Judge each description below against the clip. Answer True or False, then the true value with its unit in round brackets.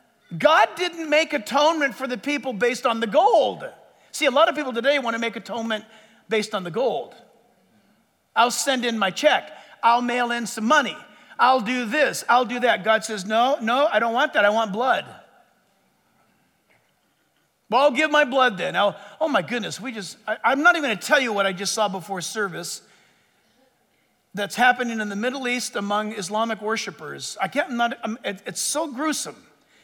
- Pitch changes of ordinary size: True (4.5 semitones)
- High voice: True (235 Hz)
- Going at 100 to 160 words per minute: False (195 wpm)